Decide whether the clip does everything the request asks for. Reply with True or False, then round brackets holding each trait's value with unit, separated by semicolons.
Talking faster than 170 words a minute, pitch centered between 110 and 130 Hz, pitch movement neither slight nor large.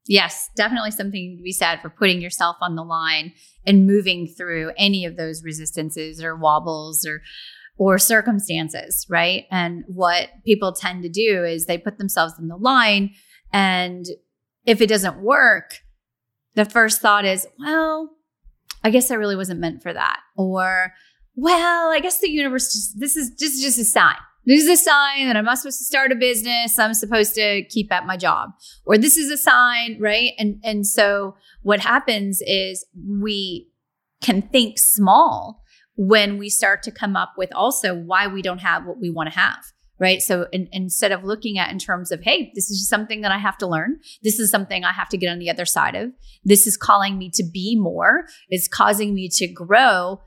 False (195 wpm; 200 Hz; 4.1 semitones)